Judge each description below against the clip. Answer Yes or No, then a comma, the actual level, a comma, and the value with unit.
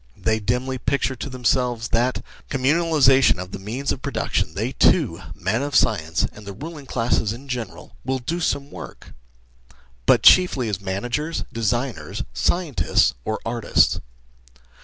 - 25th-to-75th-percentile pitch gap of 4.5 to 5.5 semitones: No, average, 4.0 semitones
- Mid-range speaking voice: No, low, 125 Hz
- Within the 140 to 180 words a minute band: Yes, average, 155 wpm